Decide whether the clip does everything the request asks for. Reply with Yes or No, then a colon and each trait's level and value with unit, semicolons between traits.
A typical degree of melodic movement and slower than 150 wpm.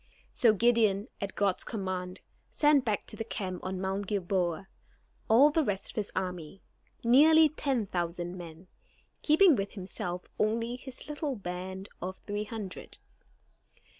Yes: average, 4.5 semitones; average, 140 wpm